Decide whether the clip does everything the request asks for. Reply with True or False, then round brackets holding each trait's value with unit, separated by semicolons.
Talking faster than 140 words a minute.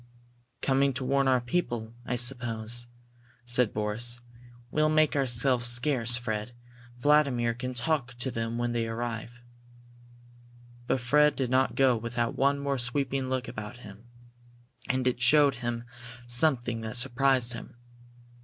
False (135 wpm)